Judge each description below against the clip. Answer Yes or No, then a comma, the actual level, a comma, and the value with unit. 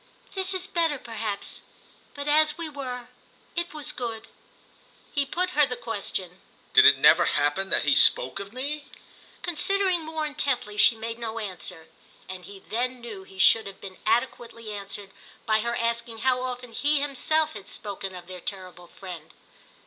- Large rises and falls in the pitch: Yes, wide, 6.8 semitones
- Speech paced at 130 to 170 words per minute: Yes, average, 165 wpm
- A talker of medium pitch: No, high, 235 Hz